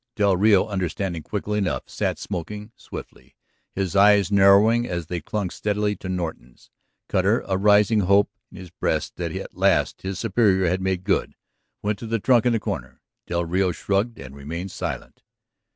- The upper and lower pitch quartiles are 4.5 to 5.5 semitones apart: No, average, 2.7 semitones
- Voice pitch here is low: Yes, low, 100 Hz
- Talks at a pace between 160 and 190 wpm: Yes, average, 170 wpm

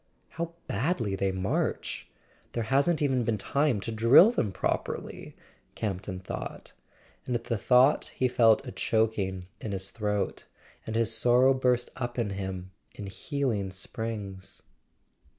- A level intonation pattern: No, average, 4.4 semitones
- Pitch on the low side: Yes, low, 115 Hz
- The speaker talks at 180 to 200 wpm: No, slow, 135 wpm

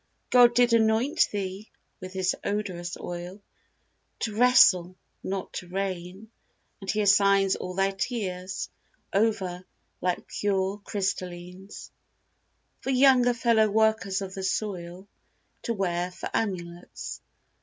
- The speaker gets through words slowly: Yes, slow, 115 wpm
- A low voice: No, high, 195 Hz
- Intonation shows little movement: No, average, 3.1 semitones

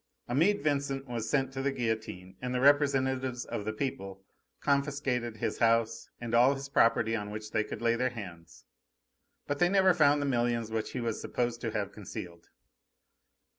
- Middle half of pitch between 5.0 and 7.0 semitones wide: No, average, 3.8 semitones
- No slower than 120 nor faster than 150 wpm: No, average, 175 wpm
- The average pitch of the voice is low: Yes, low, 120 Hz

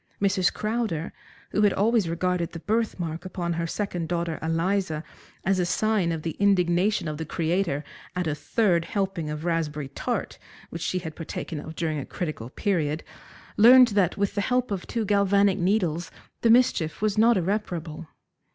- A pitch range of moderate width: Yes, average, 3.8 semitones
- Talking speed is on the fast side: No, average, 170 wpm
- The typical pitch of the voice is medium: Yes, medium, 180 Hz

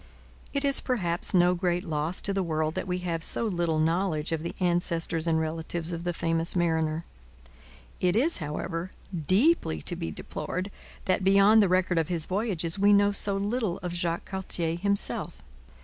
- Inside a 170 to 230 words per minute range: Yes, average, 175 wpm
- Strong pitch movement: No, average, 3.1 semitones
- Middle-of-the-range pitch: Yes, medium, 175 Hz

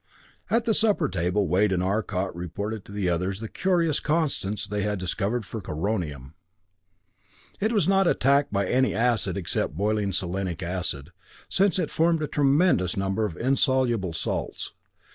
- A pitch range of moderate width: No, wide, 6.9 semitones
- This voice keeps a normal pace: Yes, average, 155 wpm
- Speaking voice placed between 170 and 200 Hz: No, low, 105 Hz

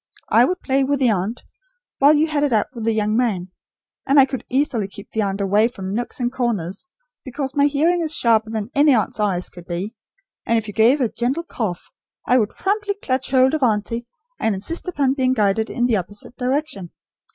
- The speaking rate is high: Yes, fast, 210 wpm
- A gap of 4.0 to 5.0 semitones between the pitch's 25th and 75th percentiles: Yes, average, 4.7 semitones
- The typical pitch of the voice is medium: No, high, 240 Hz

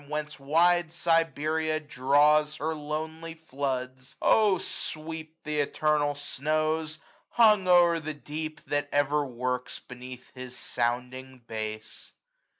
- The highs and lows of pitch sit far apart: No, average, 3.4 semitones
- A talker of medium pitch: Yes, medium, 150 Hz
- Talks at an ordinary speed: No, slow, 105 wpm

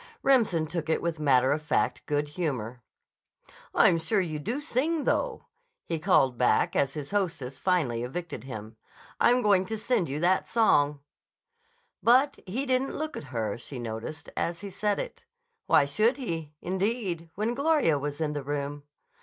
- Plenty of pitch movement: Yes, wide, 7.2 semitones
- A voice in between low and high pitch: Yes, medium, 165 Hz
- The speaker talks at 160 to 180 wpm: Yes, average, 165 wpm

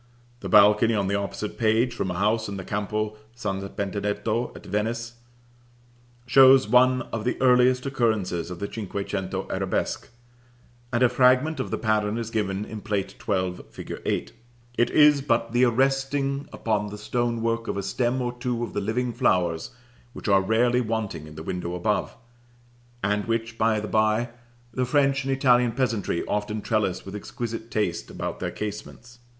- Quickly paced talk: No, average, 170 wpm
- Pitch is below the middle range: Yes, low, 110 Hz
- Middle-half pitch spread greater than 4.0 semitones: No, average, 3.3 semitones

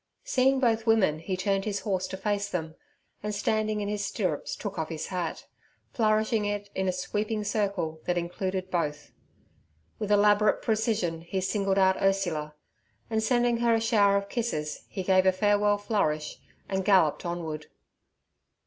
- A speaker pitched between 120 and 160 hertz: No, high, 200 Hz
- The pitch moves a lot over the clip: No, average, 2.9 semitones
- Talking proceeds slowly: No, average, 160 wpm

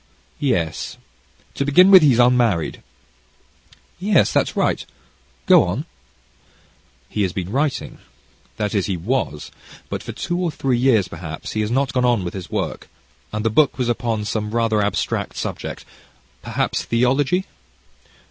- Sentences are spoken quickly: No, average, 150 wpm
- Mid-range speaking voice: No, low, 115 Hz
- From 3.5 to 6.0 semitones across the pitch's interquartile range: Yes, average, 4.8 semitones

